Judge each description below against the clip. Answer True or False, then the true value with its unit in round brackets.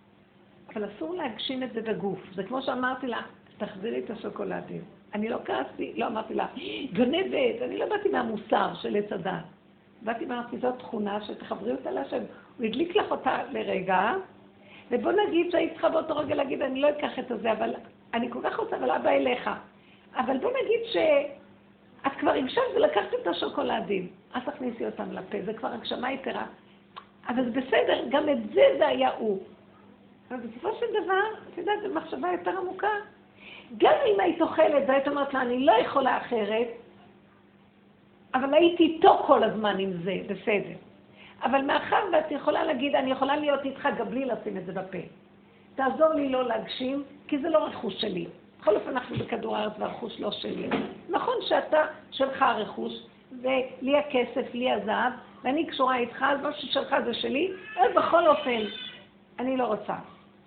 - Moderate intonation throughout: False (5.7 semitones)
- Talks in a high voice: True (265 Hz)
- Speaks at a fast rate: True (165 wpm)